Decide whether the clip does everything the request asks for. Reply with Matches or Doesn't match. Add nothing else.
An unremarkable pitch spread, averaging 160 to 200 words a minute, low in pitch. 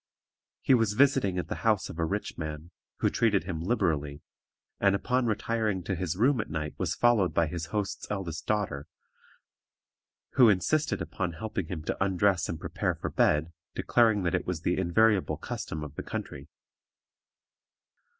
Matches